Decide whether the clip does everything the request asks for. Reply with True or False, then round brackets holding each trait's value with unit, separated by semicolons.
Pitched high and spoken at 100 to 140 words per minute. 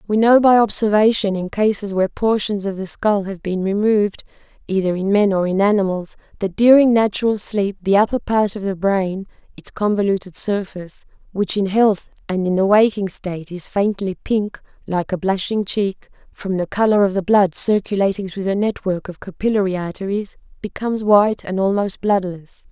False (200 Hz; 170 wpm)